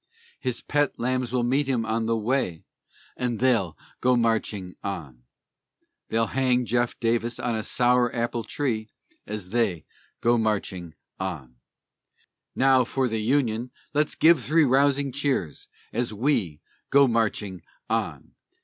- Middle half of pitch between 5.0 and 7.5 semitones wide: No, average, 3.3 semitones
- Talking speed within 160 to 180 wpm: No, slow, 135 wpm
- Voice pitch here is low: Yes, low, 120 Hz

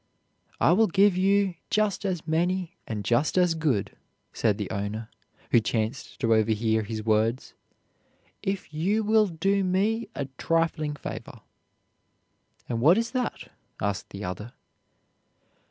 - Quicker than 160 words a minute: No, slow, 135 wpm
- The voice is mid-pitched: Yes, medium, 160 Hz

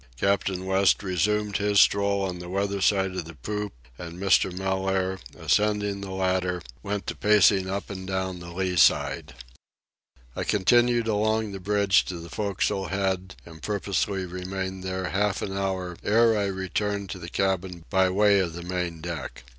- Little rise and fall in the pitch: Yes, narrow, 1.7 semitones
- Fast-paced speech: No, average, 170 wpm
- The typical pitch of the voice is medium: No, very low, 95 Hz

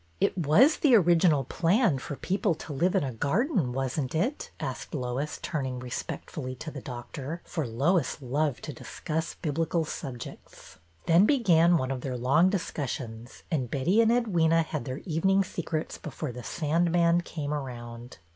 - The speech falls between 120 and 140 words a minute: No, average, 170 wpm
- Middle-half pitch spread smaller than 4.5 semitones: No, average, 5.0 semitones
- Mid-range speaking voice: Yes, medium, 155 Hz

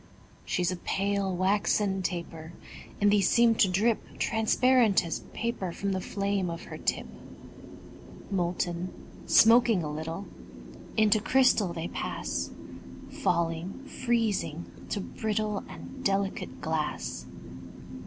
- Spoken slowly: Yes, slow, 115 wpm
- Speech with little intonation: No, average, 3.9 semitones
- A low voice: No, high, 195 Hz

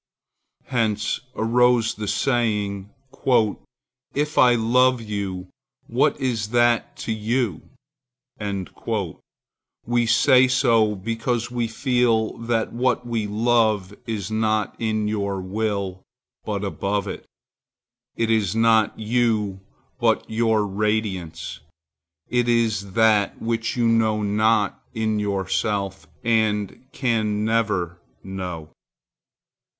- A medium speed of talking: No, slow, 105 wpm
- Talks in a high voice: No, low, 110 Hz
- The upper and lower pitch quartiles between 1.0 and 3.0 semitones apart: Yes, narrow, 2.4 semitones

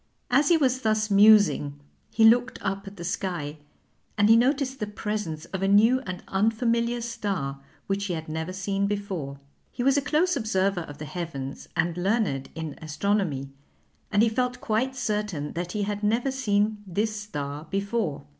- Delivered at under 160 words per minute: No, average, 175 wpm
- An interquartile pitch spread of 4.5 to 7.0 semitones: Yes, average, 4.9 semitones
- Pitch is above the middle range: Yes, high, 205 Hz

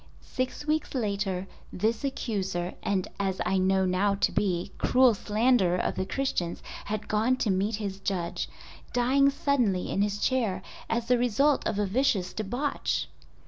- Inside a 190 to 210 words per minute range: No, average, 150 wpm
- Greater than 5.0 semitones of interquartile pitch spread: No, average, 4.6 semitones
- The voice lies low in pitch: No, high, 210 Hz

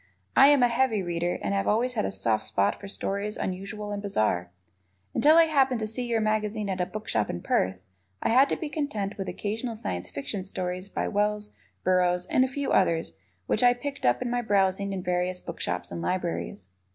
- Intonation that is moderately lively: Yes, average, 4.7 semitones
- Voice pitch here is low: No, high, 200 Hz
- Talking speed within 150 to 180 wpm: No, fast, 205 wpm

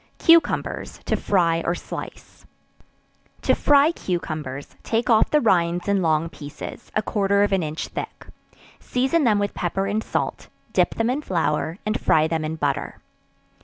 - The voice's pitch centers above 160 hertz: Yes, high, 190 Hz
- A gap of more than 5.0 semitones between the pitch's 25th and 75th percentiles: Yes, wide, 5.4 semitones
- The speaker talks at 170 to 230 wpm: No, average, 160 wpm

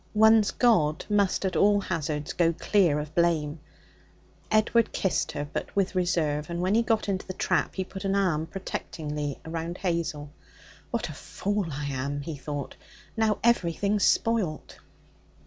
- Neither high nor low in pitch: Yes, medium, 175 Hz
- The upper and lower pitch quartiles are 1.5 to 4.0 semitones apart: No, average, 5.0 semitones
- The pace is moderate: Yes, average, 155 wpm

